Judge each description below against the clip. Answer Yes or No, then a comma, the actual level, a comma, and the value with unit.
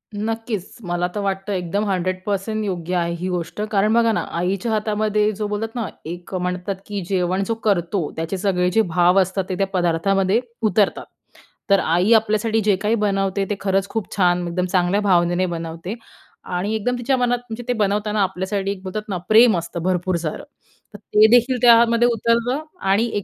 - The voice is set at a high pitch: Yes, high, 195 Hz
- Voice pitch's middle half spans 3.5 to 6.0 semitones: No, average, 3.1 semitones